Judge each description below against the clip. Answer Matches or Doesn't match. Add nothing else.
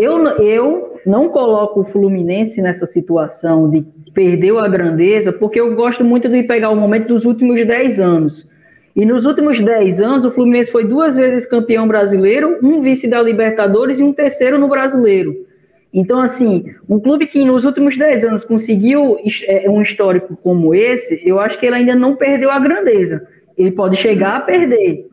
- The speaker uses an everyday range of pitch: Matches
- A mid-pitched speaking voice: Doesn't match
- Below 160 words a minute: Doesn't match